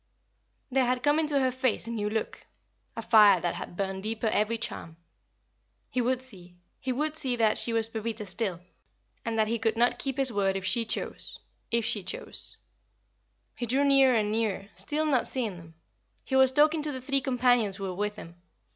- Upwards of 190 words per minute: Yes, average, 200 wpm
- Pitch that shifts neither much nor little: Yes, average, 3.9 semitones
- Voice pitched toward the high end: Yes, high, 230 Hz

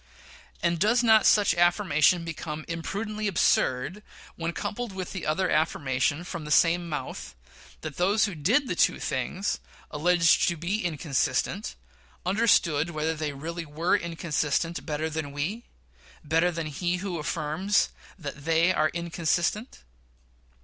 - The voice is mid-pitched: Yes, medium, 170 Hz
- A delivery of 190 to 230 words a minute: No, slow, 135 wpm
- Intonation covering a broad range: No, average, 3.4 semitones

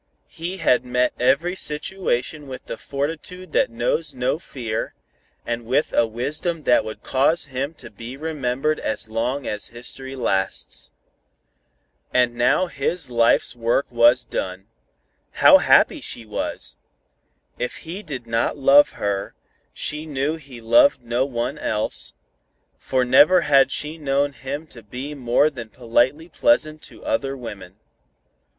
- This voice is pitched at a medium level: No, low, 130 Hz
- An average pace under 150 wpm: Yes, average, 140 wpm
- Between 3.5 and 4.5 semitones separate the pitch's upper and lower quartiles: Yes, average, 4.2 semitones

